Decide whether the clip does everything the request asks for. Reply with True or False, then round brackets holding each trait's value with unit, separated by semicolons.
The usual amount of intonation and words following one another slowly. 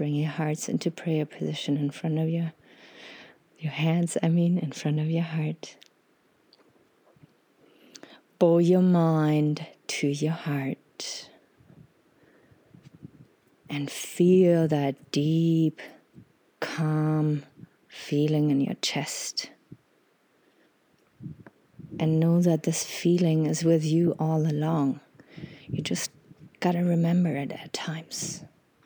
False (1.9 semitones; 110 wpm)